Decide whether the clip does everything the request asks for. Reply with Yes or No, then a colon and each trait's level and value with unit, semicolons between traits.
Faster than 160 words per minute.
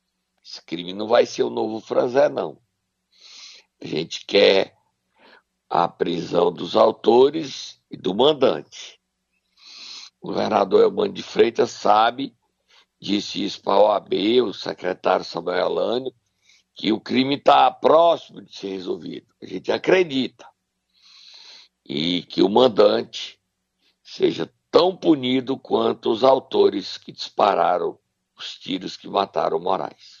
No: average, 125 wpm